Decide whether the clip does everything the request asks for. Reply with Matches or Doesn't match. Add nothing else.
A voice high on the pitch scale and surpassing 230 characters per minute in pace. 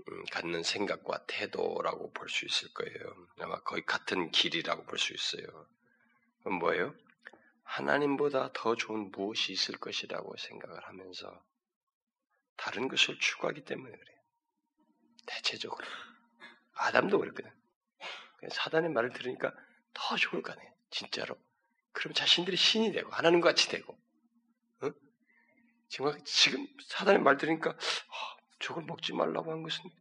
Matches